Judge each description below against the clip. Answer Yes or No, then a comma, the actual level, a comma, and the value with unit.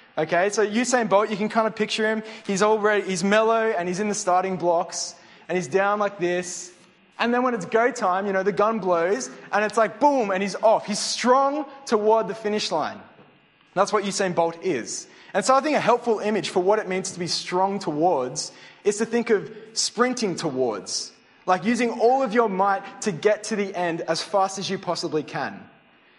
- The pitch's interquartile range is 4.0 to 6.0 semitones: No, average, 3.3 semitones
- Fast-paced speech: Yes, fast, 215 wpm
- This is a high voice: Yes, high, 205 Hz